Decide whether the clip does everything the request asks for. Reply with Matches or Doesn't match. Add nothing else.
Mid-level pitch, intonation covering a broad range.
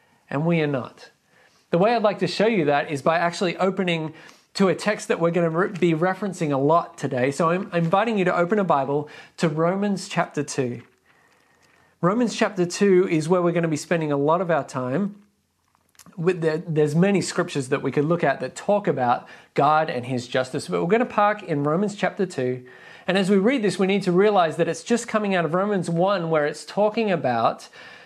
Doesn't match